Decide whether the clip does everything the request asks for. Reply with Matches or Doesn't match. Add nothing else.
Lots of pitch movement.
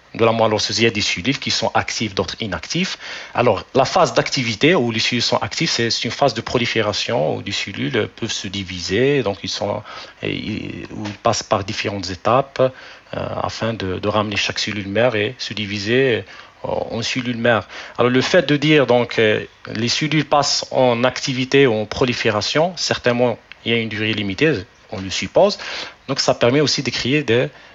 Doesn't match